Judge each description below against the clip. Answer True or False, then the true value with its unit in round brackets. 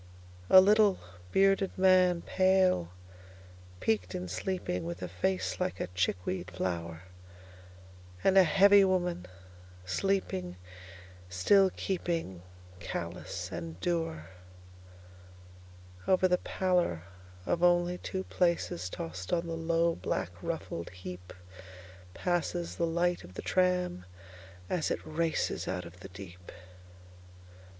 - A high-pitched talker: False (95 Hz)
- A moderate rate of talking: False (95 wpm)